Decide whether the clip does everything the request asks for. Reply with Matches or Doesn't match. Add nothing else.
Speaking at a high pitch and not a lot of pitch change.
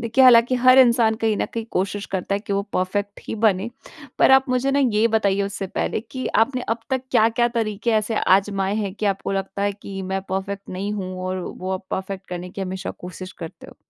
Doesn't match